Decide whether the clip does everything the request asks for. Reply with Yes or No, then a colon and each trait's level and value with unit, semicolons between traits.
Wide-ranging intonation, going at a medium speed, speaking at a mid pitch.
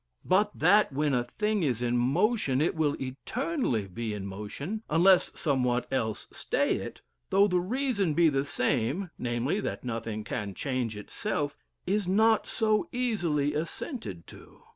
Yes: wide, 8.8 semitones; average, 150 wpm; medium, 150 Hz